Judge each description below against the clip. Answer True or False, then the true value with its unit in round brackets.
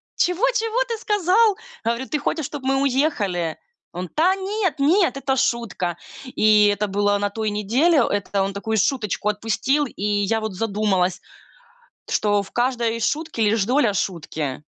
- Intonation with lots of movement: True (6.4 semitones)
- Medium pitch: False (225 Hz)